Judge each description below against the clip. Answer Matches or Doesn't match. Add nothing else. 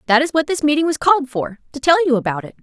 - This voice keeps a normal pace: Doesn't match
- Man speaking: Doesn't match